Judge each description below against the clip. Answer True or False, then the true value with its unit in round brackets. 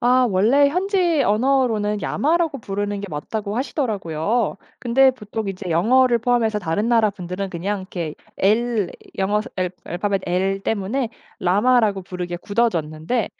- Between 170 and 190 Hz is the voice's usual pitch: False (210 Hz)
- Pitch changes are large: False (4.4 semitones)